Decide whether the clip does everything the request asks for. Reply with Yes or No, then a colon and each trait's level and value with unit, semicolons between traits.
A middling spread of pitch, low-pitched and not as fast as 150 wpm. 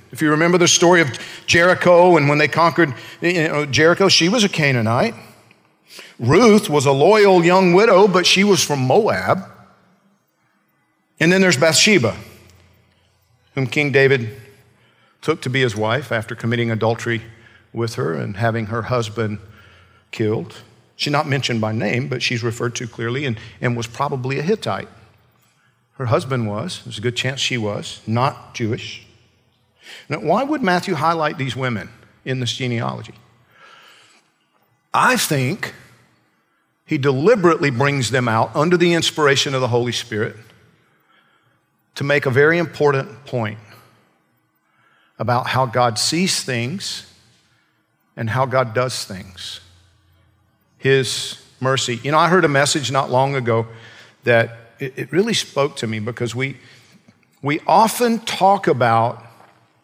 Yes: average, 4.7 semitones; low, 125 Hz; average, 140 wpm